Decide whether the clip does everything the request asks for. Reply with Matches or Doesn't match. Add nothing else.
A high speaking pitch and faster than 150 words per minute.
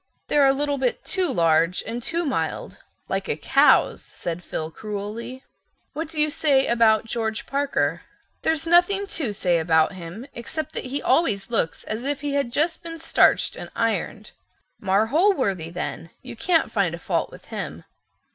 Matches